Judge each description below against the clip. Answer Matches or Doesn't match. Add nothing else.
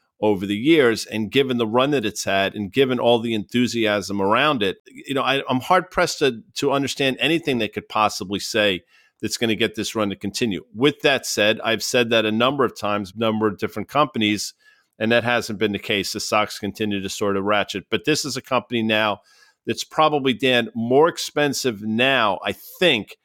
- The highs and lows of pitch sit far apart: Doesn't match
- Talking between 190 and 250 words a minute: Matches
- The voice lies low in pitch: Matches